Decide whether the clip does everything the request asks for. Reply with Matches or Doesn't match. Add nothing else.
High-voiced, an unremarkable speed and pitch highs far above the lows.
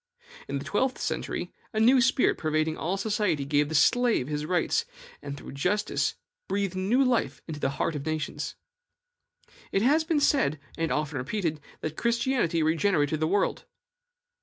Doesn't match